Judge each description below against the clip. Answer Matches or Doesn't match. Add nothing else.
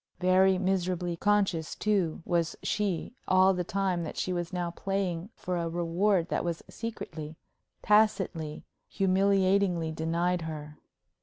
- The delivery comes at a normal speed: Doesn't match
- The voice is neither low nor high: Matches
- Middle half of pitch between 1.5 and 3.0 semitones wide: Matches